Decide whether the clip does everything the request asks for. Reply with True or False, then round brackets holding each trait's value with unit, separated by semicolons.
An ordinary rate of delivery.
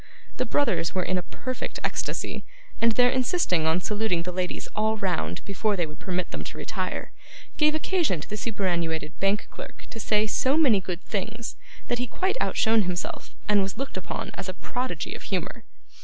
True (185 wpm)